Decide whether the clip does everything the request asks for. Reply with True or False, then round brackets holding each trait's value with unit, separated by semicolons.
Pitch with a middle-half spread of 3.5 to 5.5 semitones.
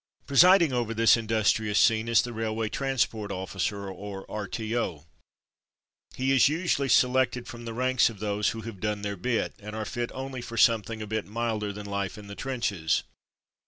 False (2.9 semitones)